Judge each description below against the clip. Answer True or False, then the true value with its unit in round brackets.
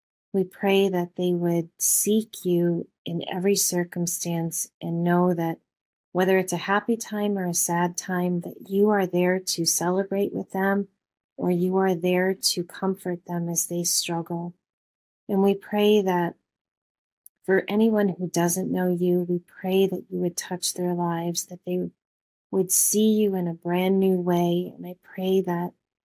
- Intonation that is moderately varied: False (1.9 semitones)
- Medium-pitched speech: True (180 Hz)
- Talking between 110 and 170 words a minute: True (165 wpm)